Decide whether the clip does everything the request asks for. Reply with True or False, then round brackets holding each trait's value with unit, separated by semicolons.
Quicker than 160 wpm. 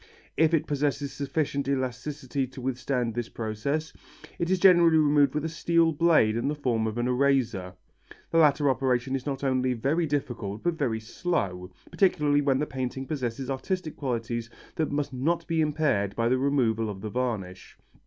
True (175 wpm)